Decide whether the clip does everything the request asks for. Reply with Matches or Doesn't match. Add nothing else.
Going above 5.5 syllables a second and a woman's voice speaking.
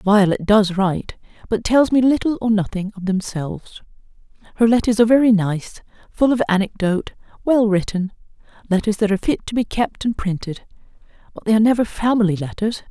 Matches